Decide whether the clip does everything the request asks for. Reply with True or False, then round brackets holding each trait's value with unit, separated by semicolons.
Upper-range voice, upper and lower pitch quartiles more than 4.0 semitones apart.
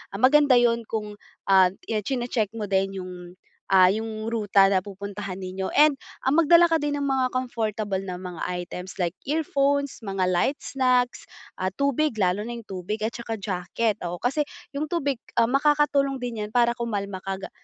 True (225 Hz; 5.6 semitones)